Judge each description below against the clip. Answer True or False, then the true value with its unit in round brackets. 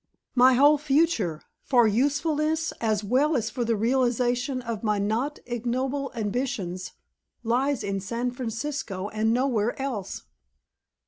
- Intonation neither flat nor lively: True (4.0 semitones)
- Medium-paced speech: False (125 wpm)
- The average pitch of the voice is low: False (245 Hz)